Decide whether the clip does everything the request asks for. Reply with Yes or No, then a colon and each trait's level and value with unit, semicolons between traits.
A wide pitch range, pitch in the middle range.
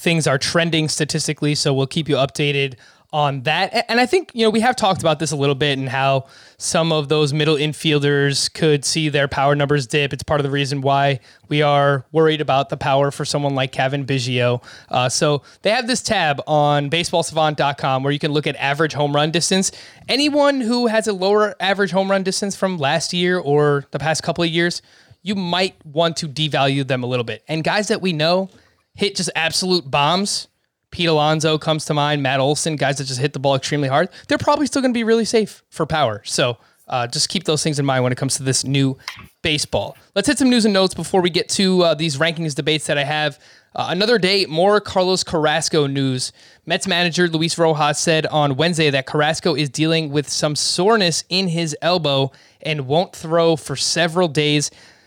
No: average, 3.8 semitones; medium, 155 Hz